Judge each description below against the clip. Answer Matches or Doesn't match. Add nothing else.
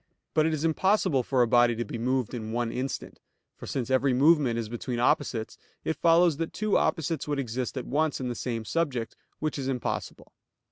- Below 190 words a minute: Doesn't match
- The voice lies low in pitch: Matches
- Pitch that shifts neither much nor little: Matches